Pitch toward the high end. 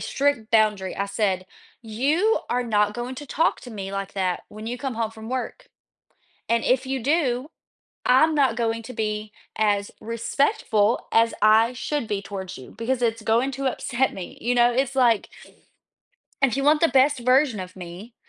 Yes: high, 230 Hz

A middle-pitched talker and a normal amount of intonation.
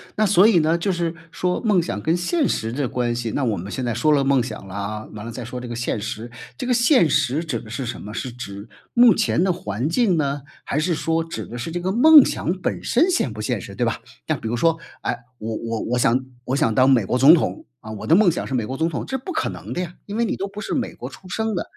No: medium, 145 Hz; wide, 7.5 semitones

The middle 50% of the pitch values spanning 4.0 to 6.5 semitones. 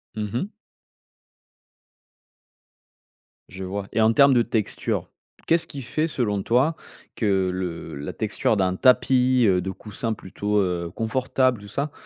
Yes: average, 5.0 semitones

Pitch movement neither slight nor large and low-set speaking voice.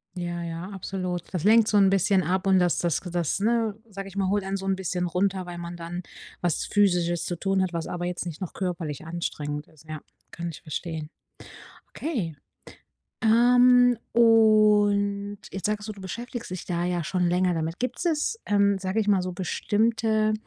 No: average, 3.1 semitones; high, 190 Hz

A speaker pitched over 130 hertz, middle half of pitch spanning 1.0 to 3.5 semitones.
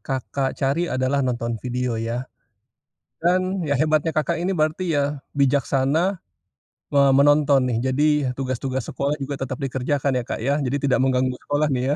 Yes: medium, 140 Hz; average, 2.7 semitones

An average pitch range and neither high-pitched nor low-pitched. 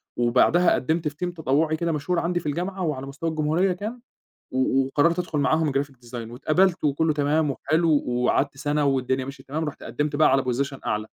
Yes: average, 3.5 semitones; medium, 150 Hz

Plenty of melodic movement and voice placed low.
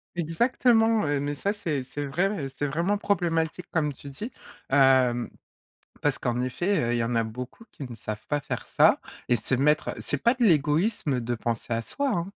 No: wide, 6.3 semitones; medium, 145 Hz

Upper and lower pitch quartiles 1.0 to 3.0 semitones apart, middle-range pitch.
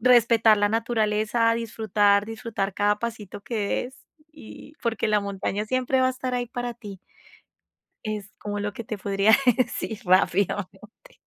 No: narrow, 2.6 semitones; high, 220 Hz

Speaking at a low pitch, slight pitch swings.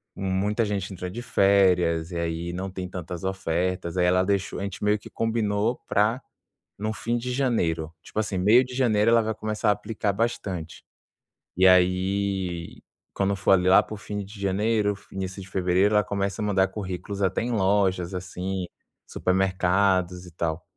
Yes: very low, 95 Hz; narrow, 2.3 semitones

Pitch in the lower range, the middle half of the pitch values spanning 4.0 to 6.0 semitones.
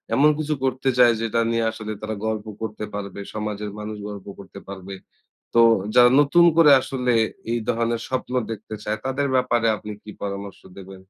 No: low, 110 Hz; average, 3.3 semitones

